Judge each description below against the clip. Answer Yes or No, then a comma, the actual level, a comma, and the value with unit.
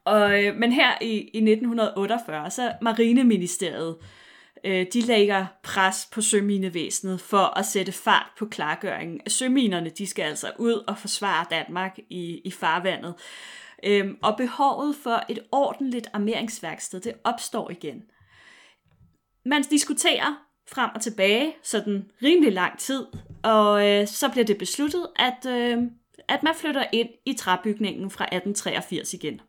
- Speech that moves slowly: Yes, slow, 120 wpm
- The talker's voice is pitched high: Yes, high, 215 Hz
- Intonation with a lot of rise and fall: No, average, 3.8 semitones